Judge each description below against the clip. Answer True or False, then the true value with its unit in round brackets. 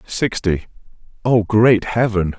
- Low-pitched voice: True (105 Hz)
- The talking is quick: False (75 wpm)